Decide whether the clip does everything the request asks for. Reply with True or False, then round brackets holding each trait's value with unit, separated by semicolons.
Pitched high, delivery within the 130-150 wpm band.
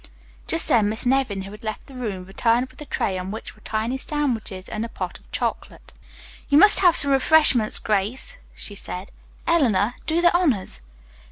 False (230 Hz; 185 wpm)